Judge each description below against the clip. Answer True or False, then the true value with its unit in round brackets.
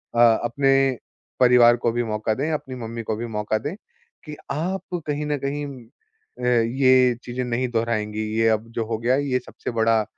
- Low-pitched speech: True (125 Hz)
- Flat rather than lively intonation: False (3.1 semitones)